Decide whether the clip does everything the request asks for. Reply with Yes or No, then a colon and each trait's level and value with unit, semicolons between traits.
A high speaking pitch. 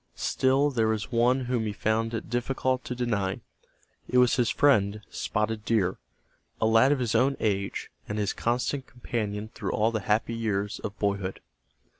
No: low, 115 Hz